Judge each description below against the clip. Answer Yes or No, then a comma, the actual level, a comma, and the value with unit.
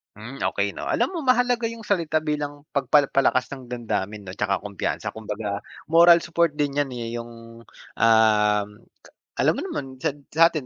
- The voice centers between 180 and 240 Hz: No, low, 135 Hz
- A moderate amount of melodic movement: No, wide, 6.8 semitones